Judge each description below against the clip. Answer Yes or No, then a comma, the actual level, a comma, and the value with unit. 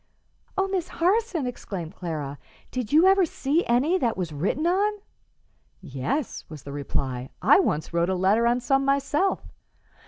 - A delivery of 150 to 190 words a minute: Yes, average, 155 wpm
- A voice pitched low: No, high, 245 Hz